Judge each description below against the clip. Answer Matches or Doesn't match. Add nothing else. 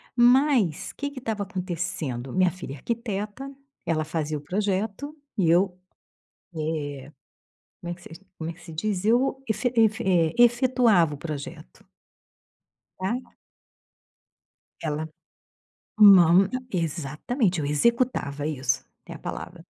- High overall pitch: Doesn't match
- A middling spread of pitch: Doesn't match